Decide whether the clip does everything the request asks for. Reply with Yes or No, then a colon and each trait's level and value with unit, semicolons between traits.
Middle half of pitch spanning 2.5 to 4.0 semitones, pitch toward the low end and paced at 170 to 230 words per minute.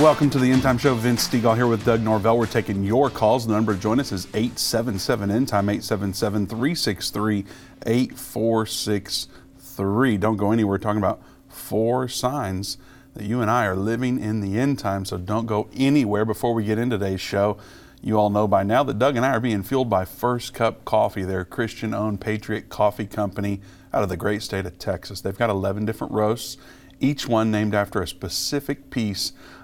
Yes: average, 3.3 semitones; low, 110 Hz; average, 190 wpm